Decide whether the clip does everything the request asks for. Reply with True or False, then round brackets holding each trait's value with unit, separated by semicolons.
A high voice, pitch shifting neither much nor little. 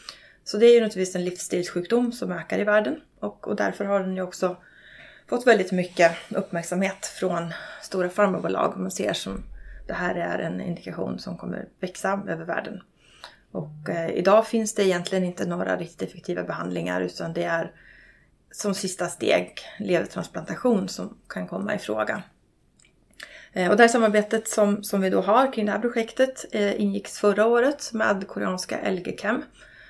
True (195 Hz; 3.2 semitones)